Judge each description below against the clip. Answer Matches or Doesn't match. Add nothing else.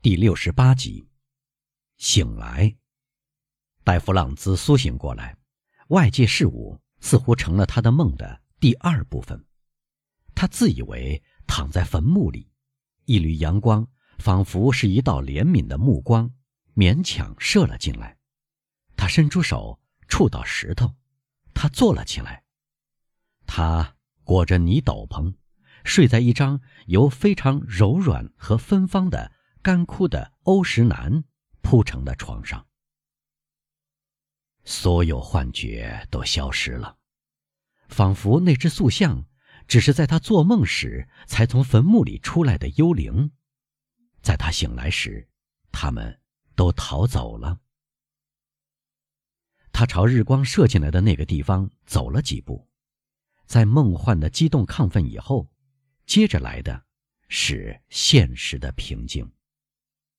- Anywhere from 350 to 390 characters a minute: Doesn't match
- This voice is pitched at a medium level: Doesn't match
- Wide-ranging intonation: Matches